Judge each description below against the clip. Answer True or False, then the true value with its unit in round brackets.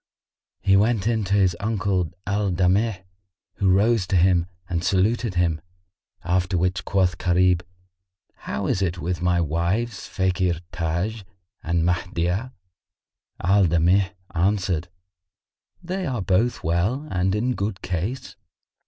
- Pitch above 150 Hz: False (95 Hz)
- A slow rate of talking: True (125 wpm)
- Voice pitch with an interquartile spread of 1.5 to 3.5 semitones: True (2.7 semitones)